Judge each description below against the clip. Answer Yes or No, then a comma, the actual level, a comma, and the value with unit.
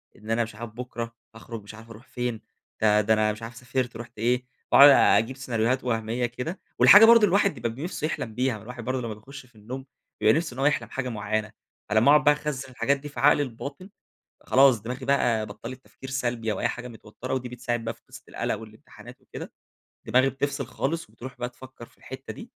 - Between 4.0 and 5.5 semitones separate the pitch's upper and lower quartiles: No, average, 3.0 semitones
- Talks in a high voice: No, low, 125 Hz